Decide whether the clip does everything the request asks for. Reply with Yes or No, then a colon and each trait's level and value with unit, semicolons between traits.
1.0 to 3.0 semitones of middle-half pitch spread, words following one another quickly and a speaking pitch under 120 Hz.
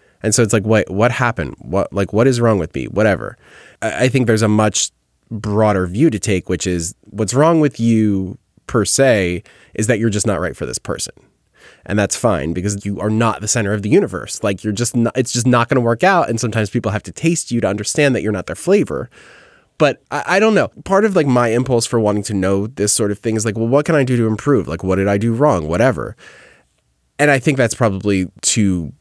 No: average, 3.4 semitones; fast, 240 wpm; low, 110 Hz